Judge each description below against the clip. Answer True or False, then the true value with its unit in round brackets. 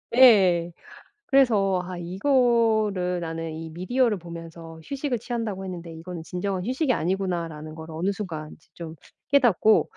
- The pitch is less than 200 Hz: True (185 Hz)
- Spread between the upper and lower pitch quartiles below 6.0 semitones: True (5.1 semitones)